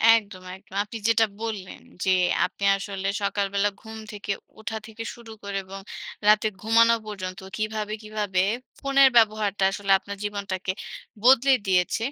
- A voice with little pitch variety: Yes, narrow, 2.2 semitones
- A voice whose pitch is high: Yes, high, 210 Hz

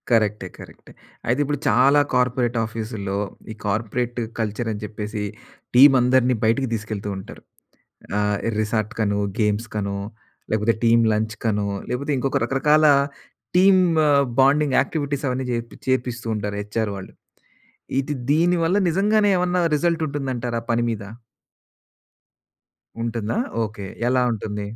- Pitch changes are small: No, average, 4.2 semitones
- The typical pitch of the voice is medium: No, low, 115 Hz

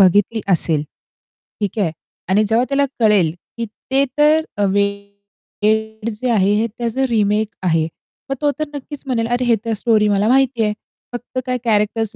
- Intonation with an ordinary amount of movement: Yes, average, 3.2 semitones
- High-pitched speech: Yes, high, 220 Hz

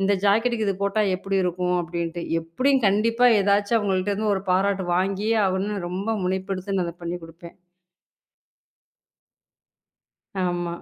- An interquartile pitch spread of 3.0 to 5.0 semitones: No, narrow, 2.6 semitones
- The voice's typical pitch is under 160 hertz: No, high, 195 Hz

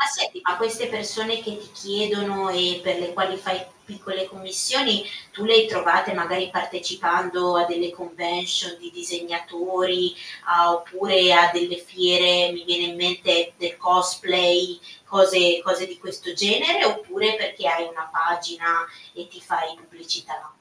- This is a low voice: No, medium, 180 Hz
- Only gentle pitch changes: Yes, narrow, 1.9 semitones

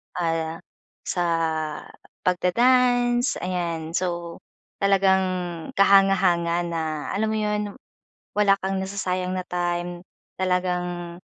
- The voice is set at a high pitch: No, medium, 180 Hz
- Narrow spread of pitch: Yes, narrow, 2.2 semitones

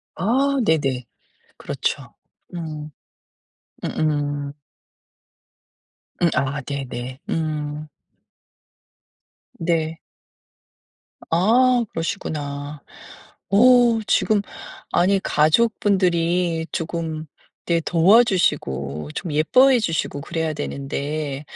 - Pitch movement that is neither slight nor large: Yes, average, 3.9 semitones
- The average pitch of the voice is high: No, medium, 160 Hz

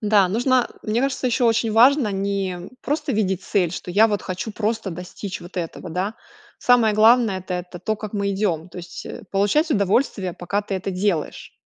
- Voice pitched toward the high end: Yes, high, 200 Hz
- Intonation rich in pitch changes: No, average, 3.5 semitones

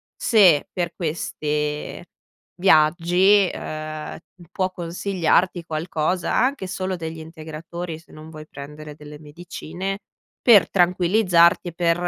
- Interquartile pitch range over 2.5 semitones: Yes, average, 2.9 semitones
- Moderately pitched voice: Yes, medium, 170 Hz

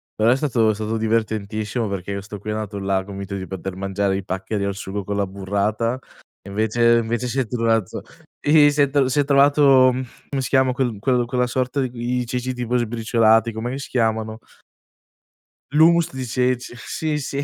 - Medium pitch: No, low, 115 Hz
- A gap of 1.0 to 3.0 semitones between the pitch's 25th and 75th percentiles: No, average, 3.8 semitones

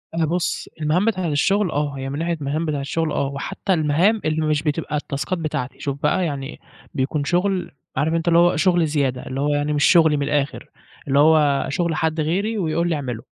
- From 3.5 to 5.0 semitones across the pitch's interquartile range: No, average, 3.0 semitones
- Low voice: No, medium, 155 Hz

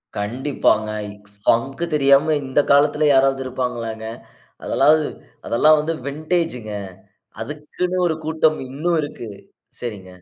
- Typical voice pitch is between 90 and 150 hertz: Yes, medium, 140 Hz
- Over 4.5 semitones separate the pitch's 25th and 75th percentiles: No, average, 4.2 semitones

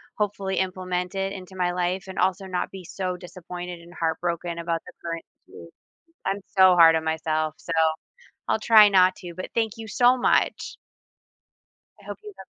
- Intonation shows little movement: Yes, narrow, 2.1 semitones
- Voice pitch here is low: No, medium, 185 Hz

